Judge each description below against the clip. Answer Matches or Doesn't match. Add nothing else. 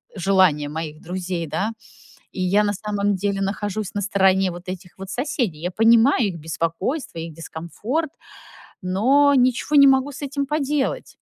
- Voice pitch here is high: Matches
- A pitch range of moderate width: Doesn't match